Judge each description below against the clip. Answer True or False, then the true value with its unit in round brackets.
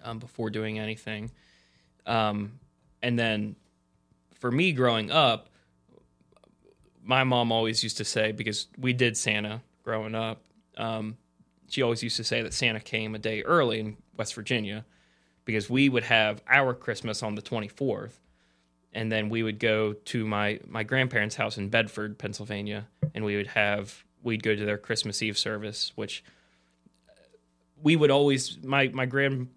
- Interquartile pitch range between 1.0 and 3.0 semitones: True (2.4 semitones)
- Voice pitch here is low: True (110 Hz)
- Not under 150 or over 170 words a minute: True (160 wpm)